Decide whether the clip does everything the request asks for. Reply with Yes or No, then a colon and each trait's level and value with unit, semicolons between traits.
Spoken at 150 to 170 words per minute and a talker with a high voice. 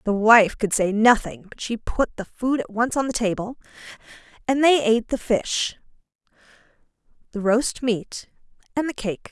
Yes: average, 165 wpm; high, 230 Hz